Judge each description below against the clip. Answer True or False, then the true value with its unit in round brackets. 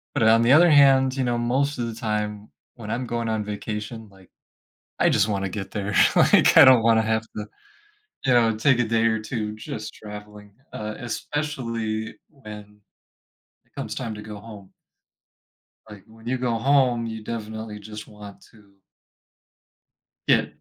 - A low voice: True (110 Hz)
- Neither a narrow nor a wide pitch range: False (2.3 semitones)